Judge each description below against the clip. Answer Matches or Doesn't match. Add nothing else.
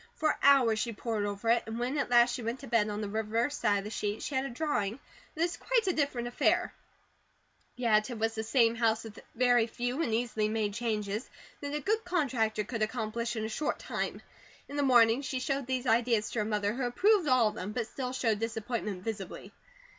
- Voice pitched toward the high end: Matches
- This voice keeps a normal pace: Doesn't match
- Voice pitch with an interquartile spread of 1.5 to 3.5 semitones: Matches